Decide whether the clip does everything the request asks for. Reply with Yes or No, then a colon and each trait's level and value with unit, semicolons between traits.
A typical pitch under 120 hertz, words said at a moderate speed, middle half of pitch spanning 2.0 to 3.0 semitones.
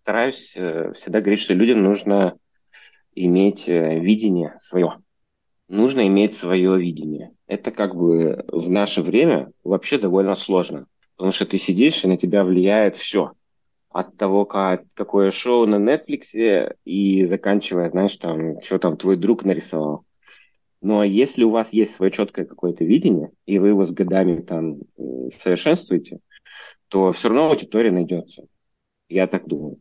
Yes: very low, 95 Hz; average, 140 wpm; narrow, 2.4 semitones